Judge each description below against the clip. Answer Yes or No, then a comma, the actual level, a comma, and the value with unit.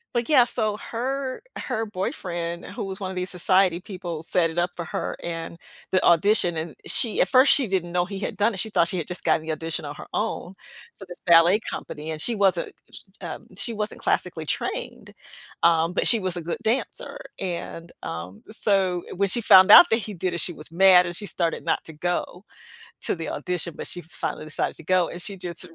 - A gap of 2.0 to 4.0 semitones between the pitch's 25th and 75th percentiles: Yes, average, 3.3 semitones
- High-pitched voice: No, medium, 180 Hz